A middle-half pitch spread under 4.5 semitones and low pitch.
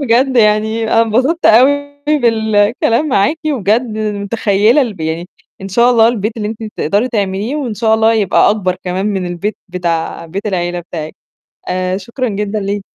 No: average, 3.3 semitones; high, 215 Hz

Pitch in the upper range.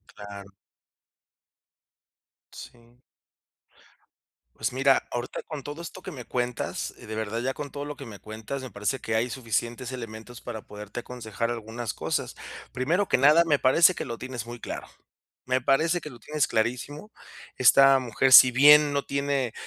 No: low, 125 Hz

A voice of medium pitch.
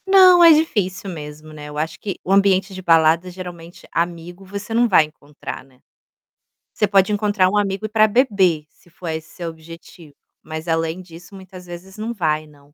Yes: medium, 180 Hz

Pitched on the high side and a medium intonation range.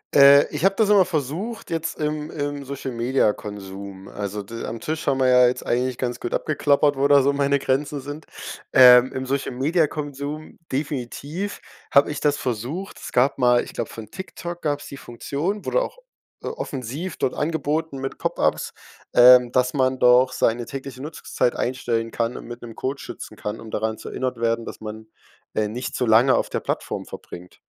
No: low, 130 Hz; average, 3.6 semitones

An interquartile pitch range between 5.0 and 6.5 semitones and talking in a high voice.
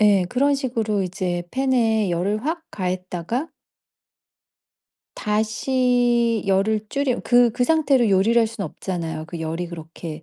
Yes: average, 5.3 semitones; high, 215 Hz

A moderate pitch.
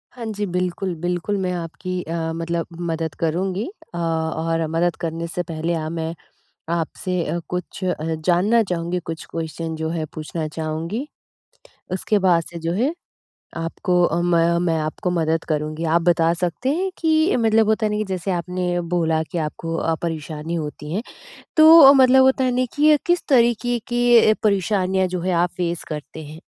Yes: medium, 175 Hz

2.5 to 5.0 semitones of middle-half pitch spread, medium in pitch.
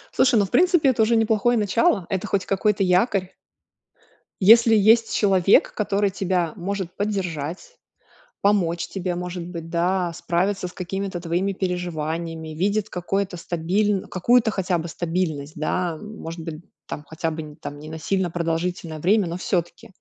Yes: average, 3.2 semitones; medium, 180 Hz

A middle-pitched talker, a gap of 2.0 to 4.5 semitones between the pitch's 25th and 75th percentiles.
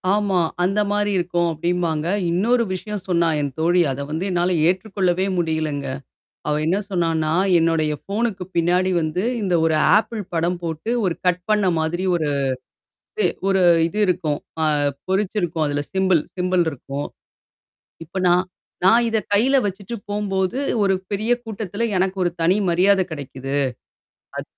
Yes: medium, 180 Hz; average, 3.3 semitones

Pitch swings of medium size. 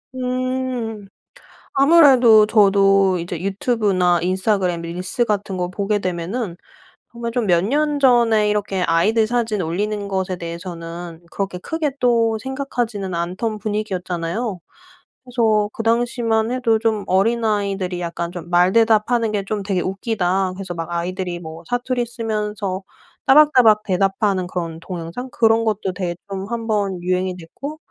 Yes: average, 4.0 semitones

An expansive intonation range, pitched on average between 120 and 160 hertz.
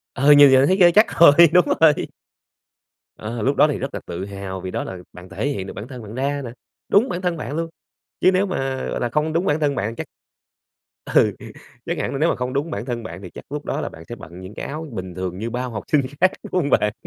Yes: wide, 6.8 semitones; low, 135 Hz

